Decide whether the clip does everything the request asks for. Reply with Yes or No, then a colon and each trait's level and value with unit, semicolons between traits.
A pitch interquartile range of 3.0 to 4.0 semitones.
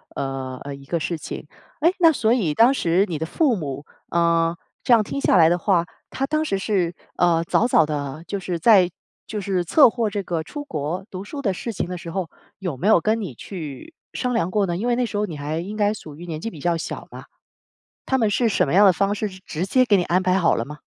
No: average, 4.8 semitones